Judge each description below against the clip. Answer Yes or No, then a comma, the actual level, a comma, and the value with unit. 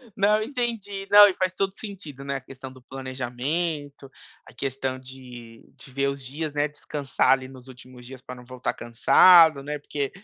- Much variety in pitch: No, average, 4.4 semitones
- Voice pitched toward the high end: No, medium, 140 Hz